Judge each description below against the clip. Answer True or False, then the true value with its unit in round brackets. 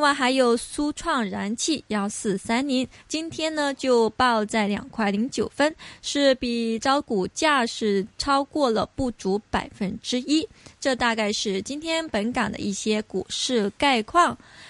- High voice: True (245 Hz)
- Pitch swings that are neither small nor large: True (4.7 semitones)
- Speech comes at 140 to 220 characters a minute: True (215 characters per minute)